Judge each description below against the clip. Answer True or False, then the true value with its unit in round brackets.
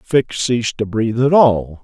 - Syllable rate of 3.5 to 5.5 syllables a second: True (4.6 syllables/s)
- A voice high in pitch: False (120 Hz)